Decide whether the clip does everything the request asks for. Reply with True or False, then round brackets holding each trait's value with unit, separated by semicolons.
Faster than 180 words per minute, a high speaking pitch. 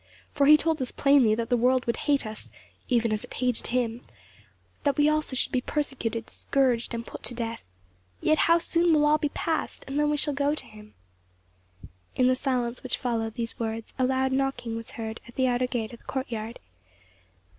True (205 wpm; 255 Hz)